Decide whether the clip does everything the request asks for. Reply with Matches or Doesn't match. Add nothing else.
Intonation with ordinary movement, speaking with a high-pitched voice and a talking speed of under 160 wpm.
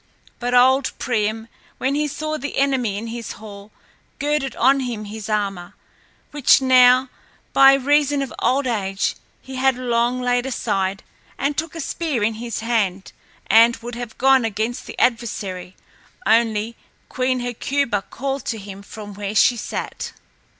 Matches